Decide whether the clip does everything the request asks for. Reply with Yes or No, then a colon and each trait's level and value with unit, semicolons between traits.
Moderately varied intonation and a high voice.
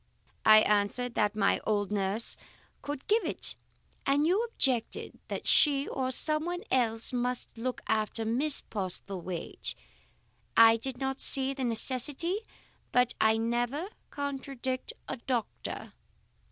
Yes: average, 3.9 semitones; very high, 250 Hz